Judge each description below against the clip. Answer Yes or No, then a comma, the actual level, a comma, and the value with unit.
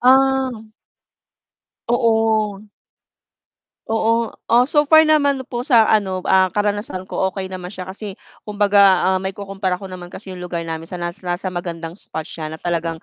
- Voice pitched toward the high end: Yes, high, 195 Hz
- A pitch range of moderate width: Yes, average, 4.1 semitones